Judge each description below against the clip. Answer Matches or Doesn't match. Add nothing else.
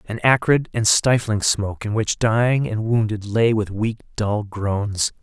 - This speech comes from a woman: Doesn't match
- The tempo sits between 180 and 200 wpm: Doesn't match